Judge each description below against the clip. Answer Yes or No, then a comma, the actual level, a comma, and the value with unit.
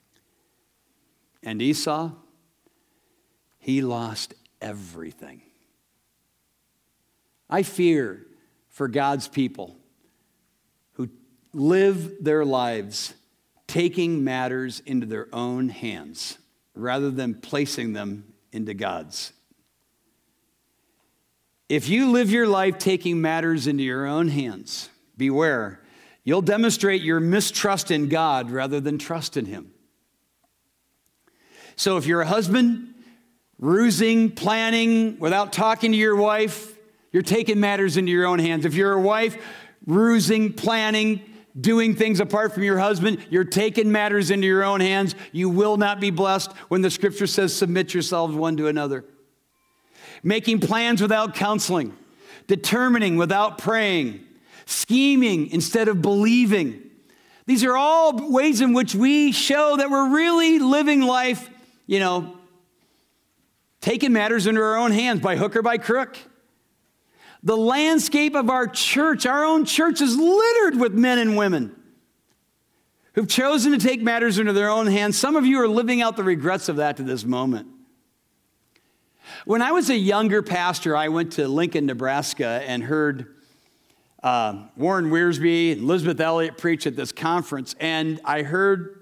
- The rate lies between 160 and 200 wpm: No, slow, 135 wpm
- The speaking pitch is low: No, high, 195 Hz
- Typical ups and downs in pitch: No, wide, 6.4 semitones